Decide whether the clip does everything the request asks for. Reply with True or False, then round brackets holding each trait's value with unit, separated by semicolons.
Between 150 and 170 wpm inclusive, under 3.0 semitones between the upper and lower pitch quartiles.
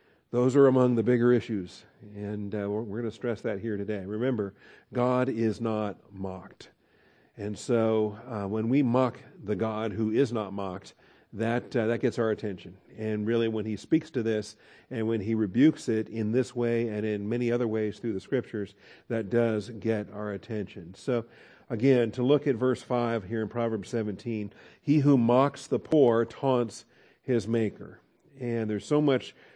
False (185 wpm; 2.5 semitones)